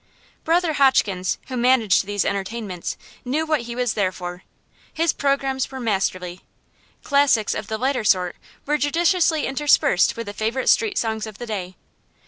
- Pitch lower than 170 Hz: No, high, 235 Hz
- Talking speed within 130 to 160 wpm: Yes, average, 155 wpm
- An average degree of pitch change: No, wide, 5.9 semitones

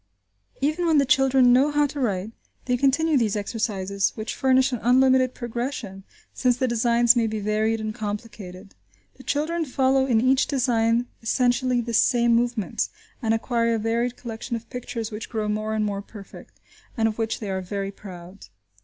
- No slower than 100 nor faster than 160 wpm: No, average, 175 wpm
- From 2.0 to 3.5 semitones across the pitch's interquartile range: Yes, average, 3.2 semitones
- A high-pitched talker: Yes, high, 235 Hz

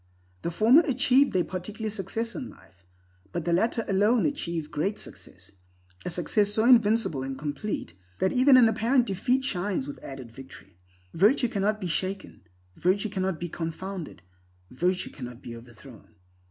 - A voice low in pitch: No, high, 190 Hz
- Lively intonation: Yes, wide, 6.6 semitones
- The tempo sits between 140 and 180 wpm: Yes, average, 155 wpm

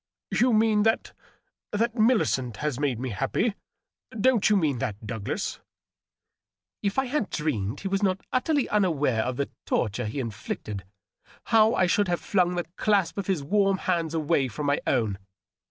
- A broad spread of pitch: Yes, wide, 8.4 semitones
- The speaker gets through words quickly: No, average, 175 wpm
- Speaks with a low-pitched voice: No, medium, 175 Hz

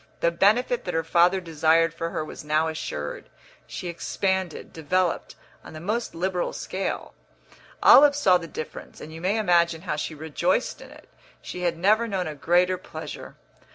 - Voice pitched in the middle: Yes, medium, 175 Hz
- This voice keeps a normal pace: Yes, average, 170 wpm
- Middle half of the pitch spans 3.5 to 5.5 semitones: No, average, 2.8 semitones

